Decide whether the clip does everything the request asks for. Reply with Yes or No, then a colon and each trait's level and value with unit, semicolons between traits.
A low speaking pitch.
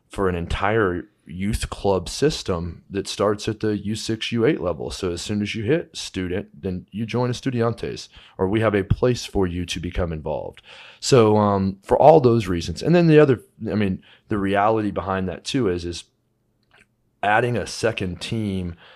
Yes: low, 100 Hz